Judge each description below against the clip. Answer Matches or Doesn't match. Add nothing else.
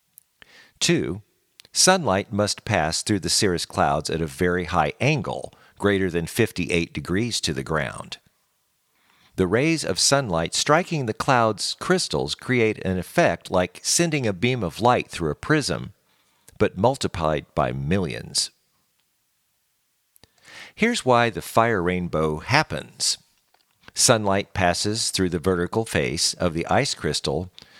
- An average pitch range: Doesn't match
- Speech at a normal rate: Doesn't match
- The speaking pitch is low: Matches